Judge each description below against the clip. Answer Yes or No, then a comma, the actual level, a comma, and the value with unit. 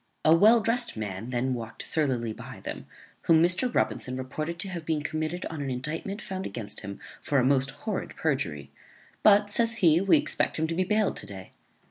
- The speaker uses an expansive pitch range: Yes, wide, 7.1 semitones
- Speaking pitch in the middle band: Yes, medium, 155 Hz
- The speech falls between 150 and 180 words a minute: No, average, 190 wpm